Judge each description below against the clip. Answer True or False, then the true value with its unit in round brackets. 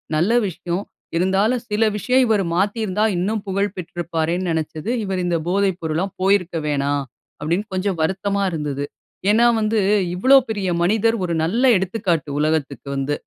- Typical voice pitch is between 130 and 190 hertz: True (185 Hz)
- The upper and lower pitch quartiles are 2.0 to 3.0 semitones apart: False (4.1 semitones)